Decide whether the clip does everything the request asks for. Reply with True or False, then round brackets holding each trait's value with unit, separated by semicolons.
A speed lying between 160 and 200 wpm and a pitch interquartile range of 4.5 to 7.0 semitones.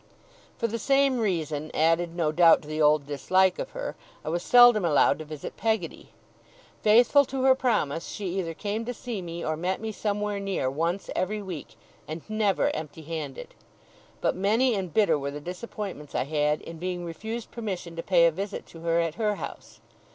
True (190 wpm; 5.2 semitones)